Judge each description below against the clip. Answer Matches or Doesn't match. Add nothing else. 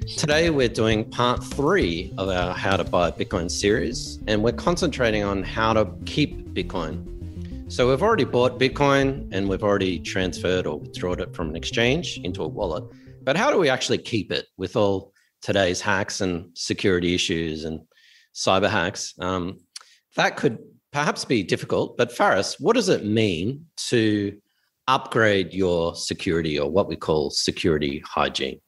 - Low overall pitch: Matches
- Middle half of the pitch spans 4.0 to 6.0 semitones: Matches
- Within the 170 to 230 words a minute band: Doesn't match